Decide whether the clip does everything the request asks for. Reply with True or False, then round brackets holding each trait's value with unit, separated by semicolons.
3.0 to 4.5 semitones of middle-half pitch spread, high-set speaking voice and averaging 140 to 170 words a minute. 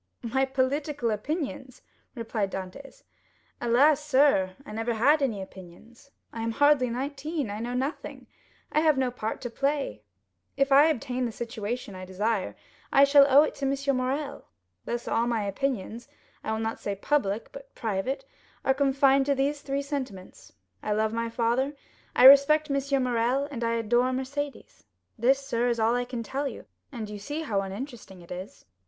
True (3.7 semitones; 255 Hz; 165 wpm)